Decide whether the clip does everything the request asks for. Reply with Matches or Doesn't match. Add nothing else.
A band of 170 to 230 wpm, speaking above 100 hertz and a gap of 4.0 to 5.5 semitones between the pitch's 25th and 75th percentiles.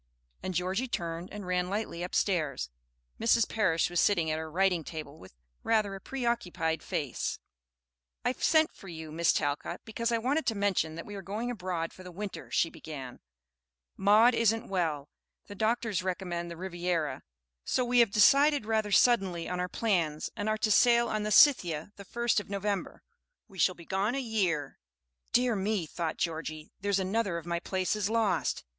Matches